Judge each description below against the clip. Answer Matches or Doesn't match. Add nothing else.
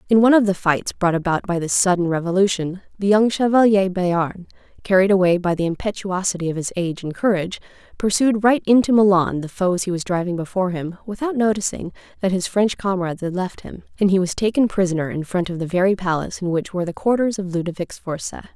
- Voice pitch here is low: Doesn't match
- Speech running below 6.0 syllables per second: Doesn't match